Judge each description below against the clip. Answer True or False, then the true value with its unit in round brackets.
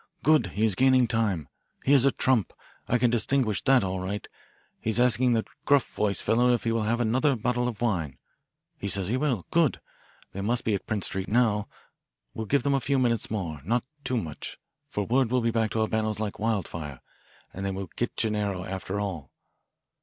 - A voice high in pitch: False (110 Hz)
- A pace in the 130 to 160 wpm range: False (200 wpm)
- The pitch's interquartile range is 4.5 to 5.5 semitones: False (3.8 semitones)